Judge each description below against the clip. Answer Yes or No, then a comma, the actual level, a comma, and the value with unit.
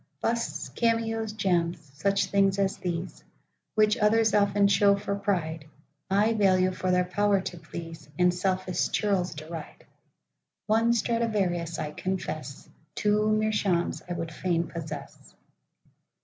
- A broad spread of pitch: No, average, 3.7 semitones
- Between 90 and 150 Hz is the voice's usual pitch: No, high, 190 Hz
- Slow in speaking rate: Yes, slow, 105 wpm